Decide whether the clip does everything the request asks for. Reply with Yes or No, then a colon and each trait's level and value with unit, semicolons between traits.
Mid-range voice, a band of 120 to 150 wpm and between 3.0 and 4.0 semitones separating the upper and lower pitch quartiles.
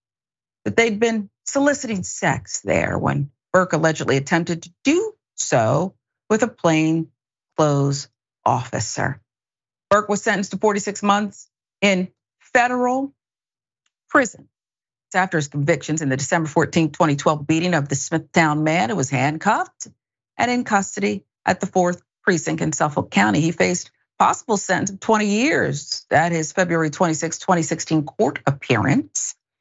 No: medium, 170 Hz; average, 140 wpm; average, 5.2 semitones